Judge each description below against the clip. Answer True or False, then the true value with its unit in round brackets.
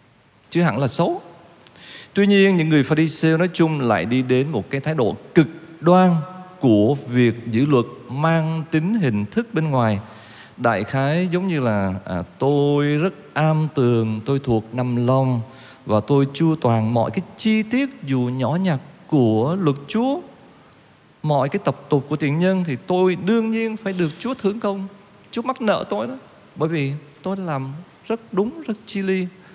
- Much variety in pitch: True (6.5 semitones)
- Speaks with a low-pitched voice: False (155 Hz)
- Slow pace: False (180 wpm)